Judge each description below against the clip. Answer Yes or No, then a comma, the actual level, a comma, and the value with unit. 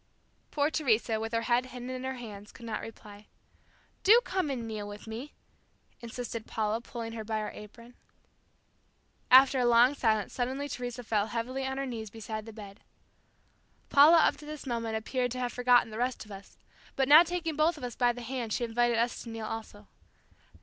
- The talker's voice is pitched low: No, high, 240 Hz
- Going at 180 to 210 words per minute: Yes, average, 200 wpm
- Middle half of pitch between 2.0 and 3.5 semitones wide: Yes, average, 2.8 semitones